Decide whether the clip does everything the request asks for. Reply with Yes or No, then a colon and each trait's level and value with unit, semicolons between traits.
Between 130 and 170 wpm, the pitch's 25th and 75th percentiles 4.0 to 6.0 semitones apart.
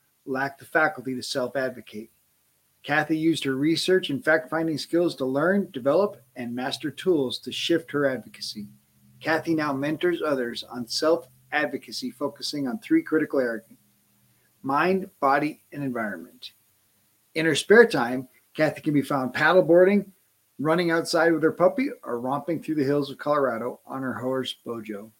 Yes: average, 150 wpm; average, 4.7 semitones